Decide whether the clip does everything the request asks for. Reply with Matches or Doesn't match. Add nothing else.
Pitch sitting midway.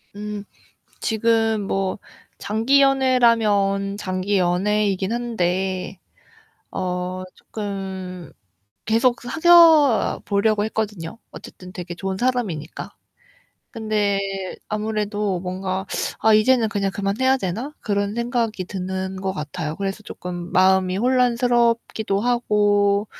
Doesn't match